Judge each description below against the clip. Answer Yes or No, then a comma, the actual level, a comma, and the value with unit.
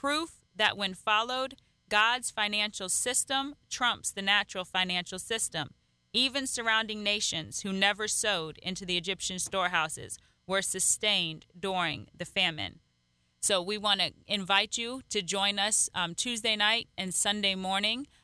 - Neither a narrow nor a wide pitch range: Yes, average, 3.0 semitones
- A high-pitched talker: Yes, high, 200 Hz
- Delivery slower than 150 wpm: Yes, average, 140 wpm